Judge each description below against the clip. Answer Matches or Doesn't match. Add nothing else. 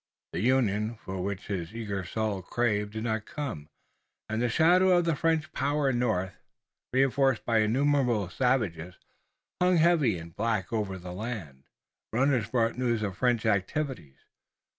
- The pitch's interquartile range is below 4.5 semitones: Doesn't match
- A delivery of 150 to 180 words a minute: Matches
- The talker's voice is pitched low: Matches